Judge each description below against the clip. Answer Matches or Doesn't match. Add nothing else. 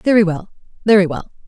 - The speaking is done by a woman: Matches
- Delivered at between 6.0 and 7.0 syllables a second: Matches